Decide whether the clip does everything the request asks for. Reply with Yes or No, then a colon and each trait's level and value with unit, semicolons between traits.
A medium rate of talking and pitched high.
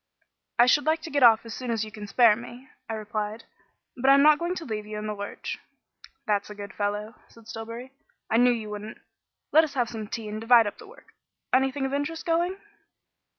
No: fast, 220 wpm; high, 230 Hz